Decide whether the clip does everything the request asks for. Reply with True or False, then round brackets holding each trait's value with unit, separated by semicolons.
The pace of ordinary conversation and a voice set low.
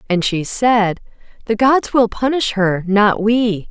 False (160 wpm; 215 Hz)